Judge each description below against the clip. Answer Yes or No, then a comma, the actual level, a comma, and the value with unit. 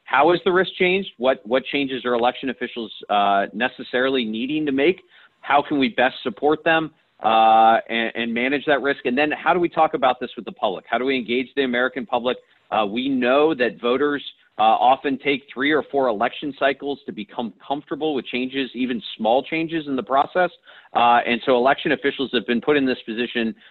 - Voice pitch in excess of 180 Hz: No, low, 130 Hz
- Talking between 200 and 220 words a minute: Yes, fast, 205 wpm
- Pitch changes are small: No, average, 3.3 semitones